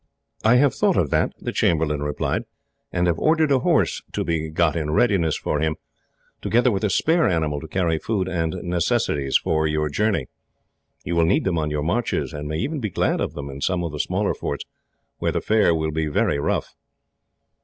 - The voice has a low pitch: Yes, very low, 80 Hz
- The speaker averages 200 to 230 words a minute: Yes, fast, 205 wpm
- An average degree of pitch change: Yes, average, 4.7 semitones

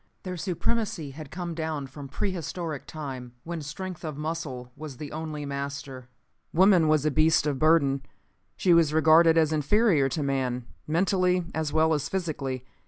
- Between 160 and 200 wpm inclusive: Yes, average, 165 wpm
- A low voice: No, medium, 155 Hz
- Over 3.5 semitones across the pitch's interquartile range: No, average, 3.1 semitones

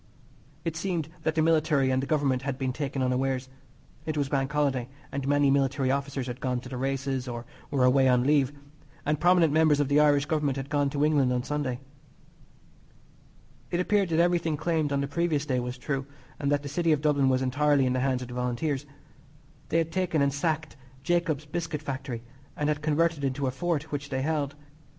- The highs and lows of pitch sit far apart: No, average, 2.7 semitones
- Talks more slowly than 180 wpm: No, fast, 205 wpm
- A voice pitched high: No, medium, 140 Hz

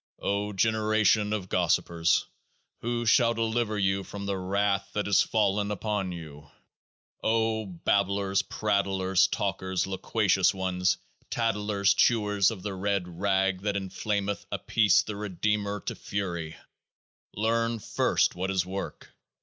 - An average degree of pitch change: No, narrow, 2.0 semitones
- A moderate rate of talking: No, slow, 125 wpm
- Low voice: Yes, low, 100 Hz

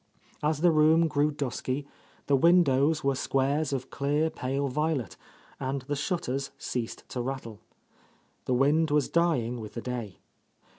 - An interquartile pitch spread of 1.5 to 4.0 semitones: Yes, average, 3.1 semitones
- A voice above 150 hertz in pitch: No, medium, 140 Hz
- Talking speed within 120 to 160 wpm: Yes, average, 145 wpm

